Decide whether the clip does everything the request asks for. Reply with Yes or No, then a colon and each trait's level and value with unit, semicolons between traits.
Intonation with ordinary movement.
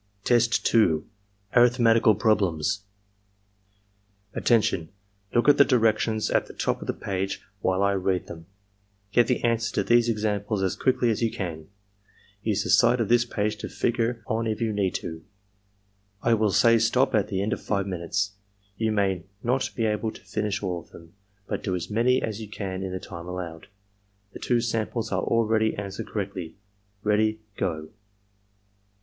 Yes: average, 3.2 semitones